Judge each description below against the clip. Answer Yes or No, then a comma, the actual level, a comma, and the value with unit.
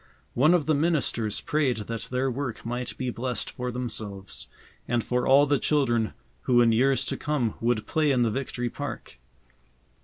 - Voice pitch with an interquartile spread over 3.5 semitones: No, average, 3.1 semitones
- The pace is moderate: Yes, average, 175 wpm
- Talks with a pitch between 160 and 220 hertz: No, low, 125 Hz